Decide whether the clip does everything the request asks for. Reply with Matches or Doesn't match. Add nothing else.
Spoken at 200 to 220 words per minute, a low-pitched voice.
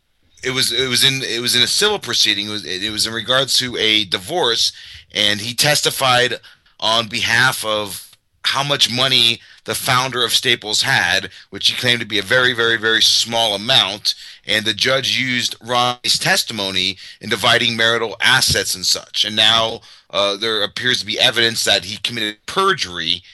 Doesn't match